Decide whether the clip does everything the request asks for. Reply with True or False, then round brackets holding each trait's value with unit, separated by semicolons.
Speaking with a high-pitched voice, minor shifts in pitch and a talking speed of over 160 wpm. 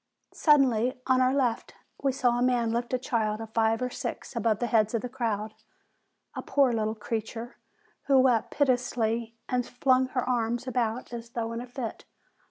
True (240 Hz; 2.1 semitones; 180 wpm)